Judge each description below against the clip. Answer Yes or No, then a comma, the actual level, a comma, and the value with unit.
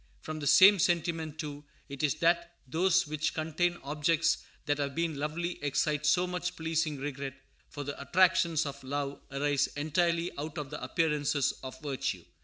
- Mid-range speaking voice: Yes, medium, 155 Hz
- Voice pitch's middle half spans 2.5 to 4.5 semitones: Yes, average, 2.8 semitones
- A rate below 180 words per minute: Yes, average, 165 wpm